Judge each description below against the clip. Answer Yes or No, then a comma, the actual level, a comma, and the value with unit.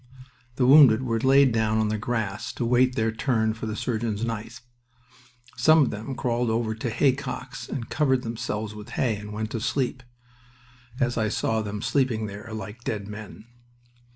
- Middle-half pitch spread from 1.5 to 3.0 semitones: Yes, narrow, 2.6 semitones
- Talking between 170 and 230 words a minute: Yes, average, 175 wpm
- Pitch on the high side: No, low, 115 Hz